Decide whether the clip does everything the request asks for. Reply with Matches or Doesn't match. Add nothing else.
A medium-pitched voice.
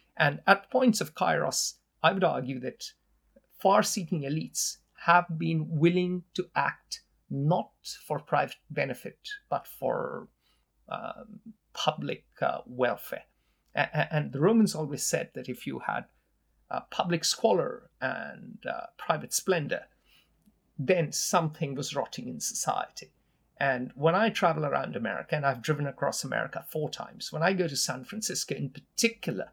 Matches